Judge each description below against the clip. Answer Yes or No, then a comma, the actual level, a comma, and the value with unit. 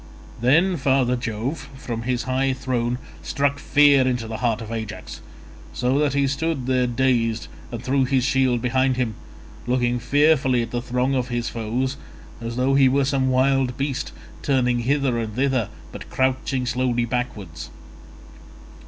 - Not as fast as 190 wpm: Yes, average, 155 wpm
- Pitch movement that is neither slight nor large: No, narrow, 2.0 semitones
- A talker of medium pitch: No, low, 130 Hz